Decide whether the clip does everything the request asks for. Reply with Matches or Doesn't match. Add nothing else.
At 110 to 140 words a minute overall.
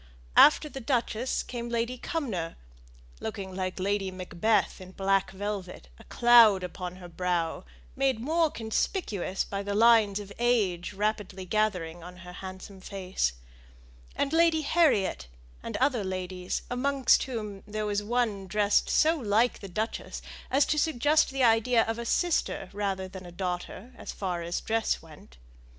Doesn't match